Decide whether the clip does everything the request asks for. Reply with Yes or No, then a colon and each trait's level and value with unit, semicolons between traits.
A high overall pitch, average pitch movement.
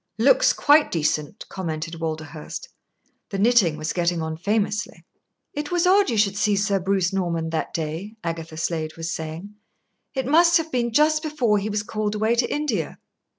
No: high, 200 Hz; wide, 6.6 semitones